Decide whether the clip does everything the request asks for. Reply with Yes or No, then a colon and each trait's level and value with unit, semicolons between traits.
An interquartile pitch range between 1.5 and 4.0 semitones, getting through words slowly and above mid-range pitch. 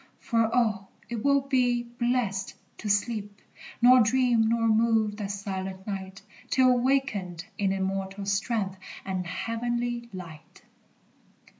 Yes: average, 3.7 semitones; slow, 120 wpm; high, 215 Hz